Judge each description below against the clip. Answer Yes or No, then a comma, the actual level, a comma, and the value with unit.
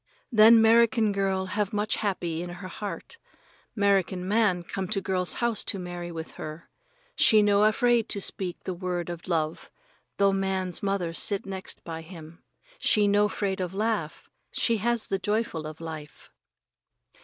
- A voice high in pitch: Yes, high, 195 Hz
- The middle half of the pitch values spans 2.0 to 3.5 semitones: Yes, average, 3.1 semitones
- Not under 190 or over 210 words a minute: No, average, 160 wpm